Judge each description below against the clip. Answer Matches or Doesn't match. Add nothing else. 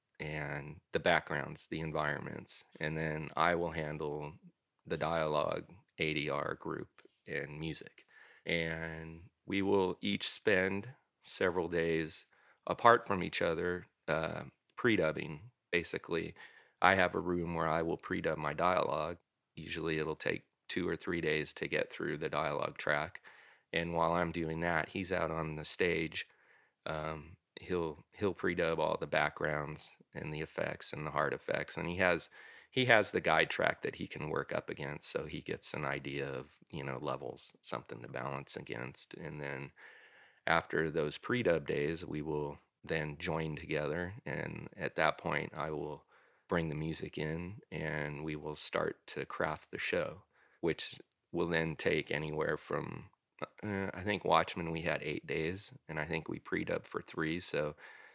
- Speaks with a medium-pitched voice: Doesn't match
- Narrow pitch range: Matches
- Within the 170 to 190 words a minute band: Doesn't match